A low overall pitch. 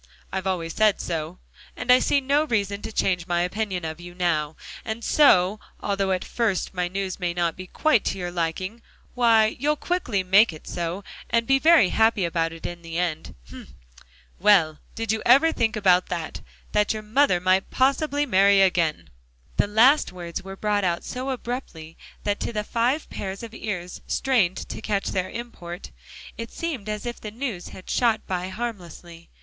No: high, 195 Hz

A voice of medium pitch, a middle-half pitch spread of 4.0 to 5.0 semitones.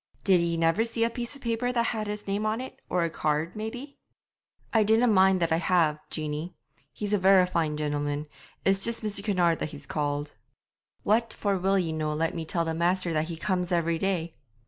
Yes: medium, 180 Hz; average, 4.7 semitones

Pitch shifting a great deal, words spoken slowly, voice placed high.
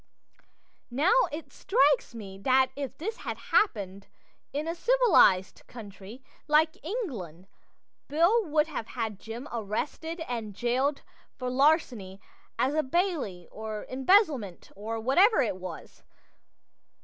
Yes: wide, 6.9 semitones; slow, 120 wpm; very high, 260 Hz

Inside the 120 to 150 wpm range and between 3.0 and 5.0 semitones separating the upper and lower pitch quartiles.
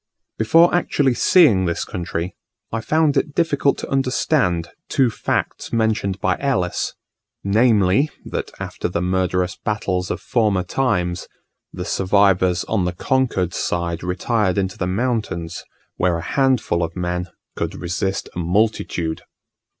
No: slow, 135 wpm; wide, 5.4 semitones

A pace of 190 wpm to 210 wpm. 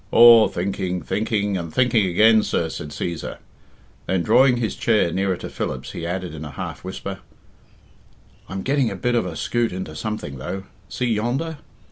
No: average, 170 wpm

